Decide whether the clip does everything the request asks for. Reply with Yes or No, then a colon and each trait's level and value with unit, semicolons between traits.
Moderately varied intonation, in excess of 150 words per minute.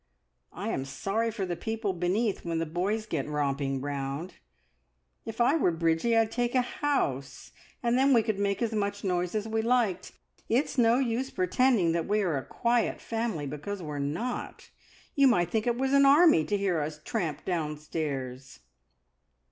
No: wide, 6.7 semitones; average, 175 wpm